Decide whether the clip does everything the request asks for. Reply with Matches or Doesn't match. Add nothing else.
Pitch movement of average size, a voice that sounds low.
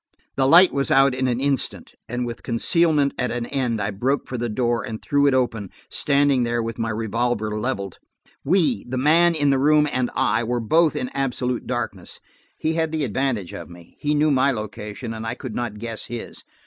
Matches